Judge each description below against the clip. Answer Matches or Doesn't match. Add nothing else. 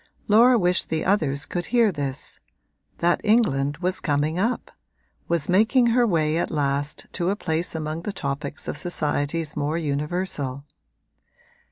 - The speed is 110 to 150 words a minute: Matches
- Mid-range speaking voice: Matches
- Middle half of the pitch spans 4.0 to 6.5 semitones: Matches